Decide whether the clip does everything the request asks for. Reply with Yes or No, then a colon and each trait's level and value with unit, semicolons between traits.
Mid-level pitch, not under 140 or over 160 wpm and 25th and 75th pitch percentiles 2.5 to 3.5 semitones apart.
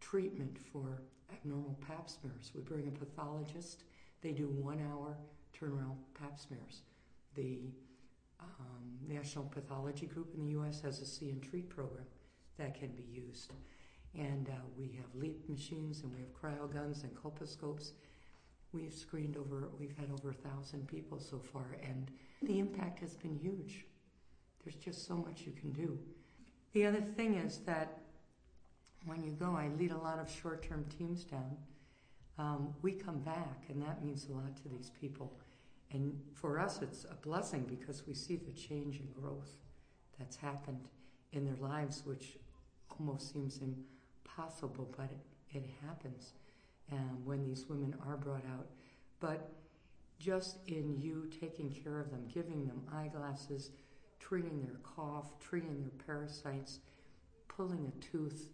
Yes: medium, 145 Hz; average, 155 wpm; average, 2.8 semitones